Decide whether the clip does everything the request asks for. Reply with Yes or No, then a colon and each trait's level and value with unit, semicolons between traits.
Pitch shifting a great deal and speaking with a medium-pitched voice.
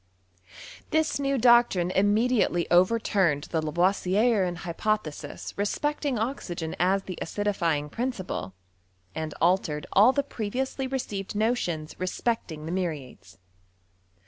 No: wide, 5.8 semitones; high, 195 Hz